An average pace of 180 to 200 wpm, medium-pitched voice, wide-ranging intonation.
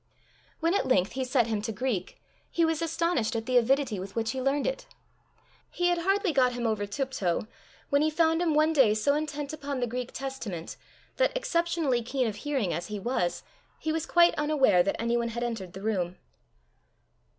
No: average, 195 wpm; very high, 260 Hz; wide, 5.9 semitones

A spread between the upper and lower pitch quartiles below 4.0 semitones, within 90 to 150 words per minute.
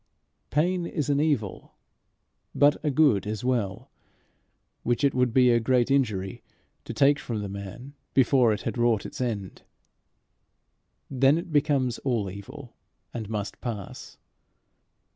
No: average, 4.7 semitones; average, 140 wpm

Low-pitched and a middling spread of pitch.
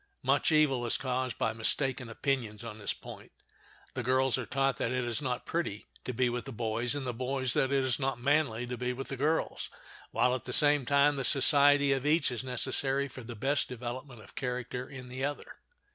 No: low, 130 Hz; narrow, 2.2 semitones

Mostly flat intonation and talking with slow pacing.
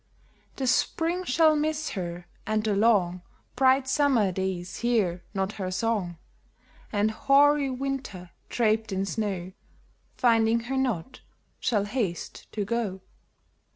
No: wide, 5.5 semitones; slow, 130 wpm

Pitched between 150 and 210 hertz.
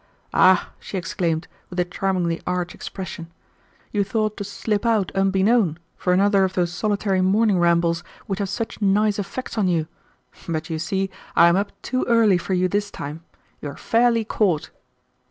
Yes: high, 190 Hz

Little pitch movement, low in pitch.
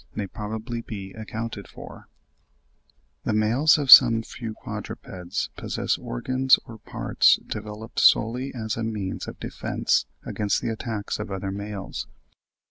Yes: narrow, 2.3 semitones; low, 110 Hz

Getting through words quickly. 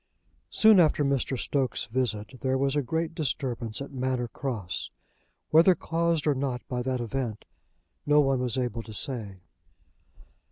No: average, 150 wpm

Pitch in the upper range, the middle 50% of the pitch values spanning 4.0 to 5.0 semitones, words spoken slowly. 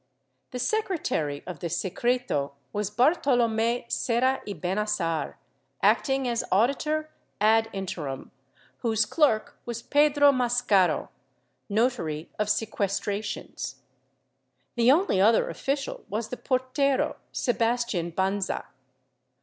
Yes: high, 225 Hz; average, 4.7 semitones; slow, 100 wpm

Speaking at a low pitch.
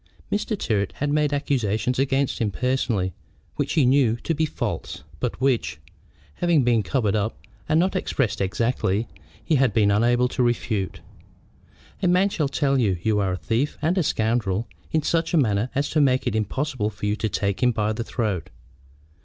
Yes: low, 120 Hz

